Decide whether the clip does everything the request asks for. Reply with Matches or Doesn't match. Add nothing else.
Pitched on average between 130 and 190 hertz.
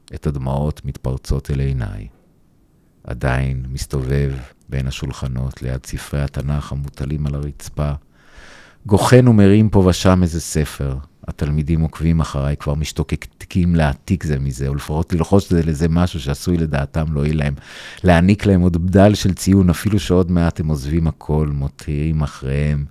Doesn't match